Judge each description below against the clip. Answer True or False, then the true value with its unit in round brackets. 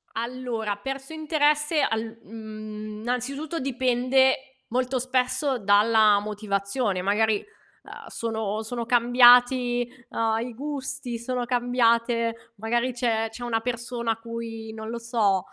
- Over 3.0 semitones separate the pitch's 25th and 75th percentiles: False (2.4 semitones)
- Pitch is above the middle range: True (235 Hz)